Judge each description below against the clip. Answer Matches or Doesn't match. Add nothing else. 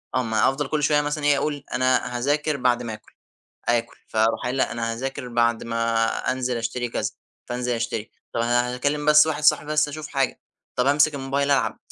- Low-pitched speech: Matches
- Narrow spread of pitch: Doesn't match